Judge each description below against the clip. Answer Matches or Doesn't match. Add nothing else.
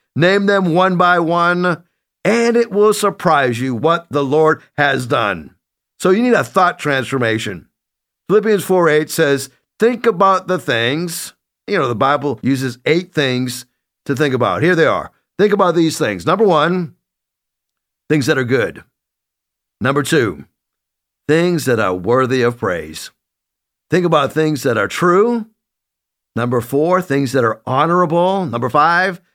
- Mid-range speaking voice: Matches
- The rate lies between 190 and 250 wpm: Doesn't match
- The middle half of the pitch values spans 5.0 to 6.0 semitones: Matches